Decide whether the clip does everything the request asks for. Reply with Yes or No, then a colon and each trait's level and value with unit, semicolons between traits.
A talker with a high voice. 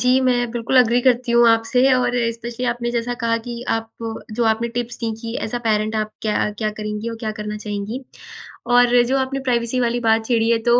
Yes: high, 235 Hz